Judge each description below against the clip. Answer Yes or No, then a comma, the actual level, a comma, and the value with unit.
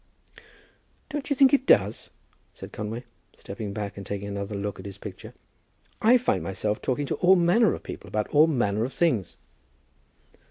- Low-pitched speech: Yes, low, 110 Hz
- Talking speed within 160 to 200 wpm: Yes, average, 170 wpm